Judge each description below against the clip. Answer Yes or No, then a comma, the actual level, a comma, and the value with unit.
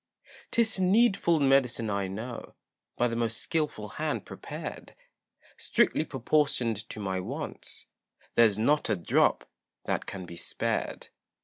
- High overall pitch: No, low, 115 Hz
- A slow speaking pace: Yes, slow, 125 wpm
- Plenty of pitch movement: Yes, wide, 6.3 semitones